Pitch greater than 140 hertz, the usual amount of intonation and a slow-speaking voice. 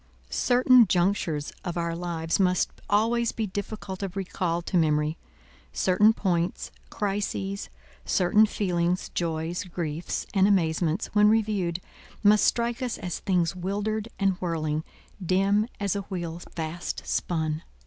Yes: medium, 185 Hz; average, 3.5 semitones; slow, 130 wpm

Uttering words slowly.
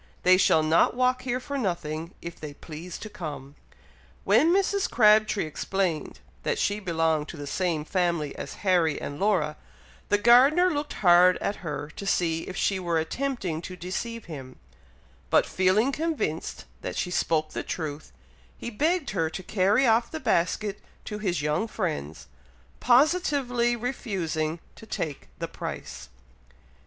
No: average, 150 wpm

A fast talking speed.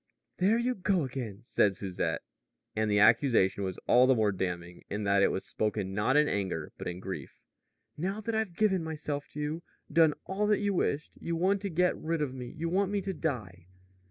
Yes: fast, 210 wpm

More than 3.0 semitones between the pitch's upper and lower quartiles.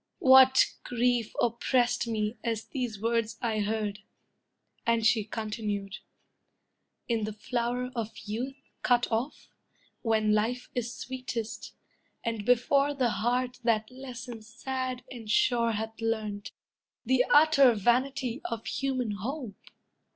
No: narrow, 2.5 semitones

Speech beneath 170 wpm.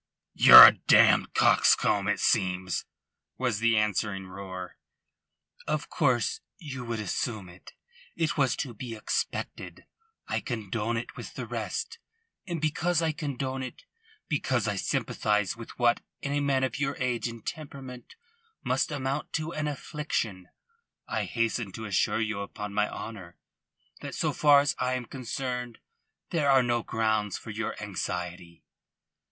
Yes: average, 145 wpm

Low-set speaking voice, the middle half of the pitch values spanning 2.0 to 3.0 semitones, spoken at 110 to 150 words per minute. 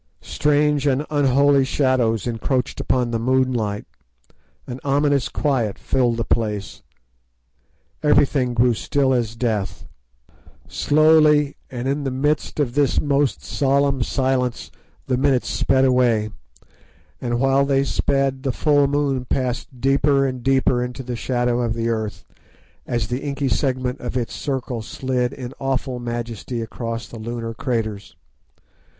Yes: low, 130 Hz; narrow, 2.6 semitones; slow, 135 wpm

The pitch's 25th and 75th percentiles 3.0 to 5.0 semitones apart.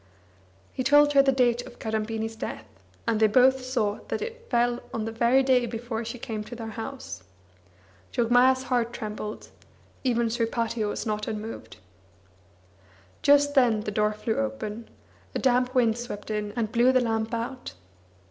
No: narrow, 2.4 semitones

